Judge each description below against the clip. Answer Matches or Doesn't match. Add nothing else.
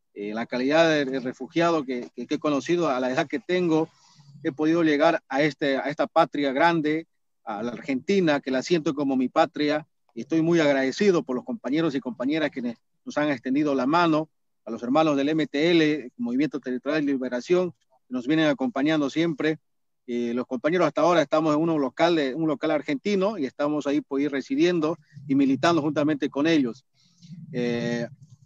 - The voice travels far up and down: Doesn't match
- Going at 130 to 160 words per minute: Doesn't match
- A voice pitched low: Doesn't match